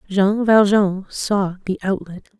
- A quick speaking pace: No, slow, 125 wpm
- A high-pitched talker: Yes, high, 195 Hz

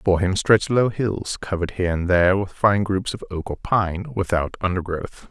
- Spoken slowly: No, fast, 205 wpm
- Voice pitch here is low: Yes, very low, 95 Hz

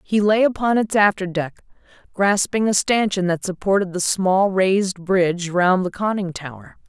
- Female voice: Yes, female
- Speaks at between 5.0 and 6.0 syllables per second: No, 4.7 syllables/s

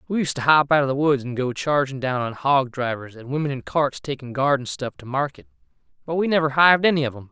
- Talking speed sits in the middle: No, fast, 255 wpm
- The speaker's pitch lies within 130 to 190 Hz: Yes, low, 135 Hz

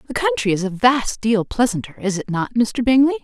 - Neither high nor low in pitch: No, high, 235 Hz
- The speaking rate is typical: No, fast, 220 wpm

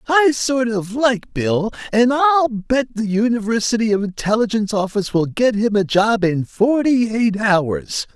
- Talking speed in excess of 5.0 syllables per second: No, 4.4 syllables/s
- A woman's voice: No, male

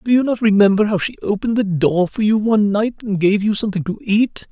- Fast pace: Yes, fast, 255 wpm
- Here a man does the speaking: Yes, male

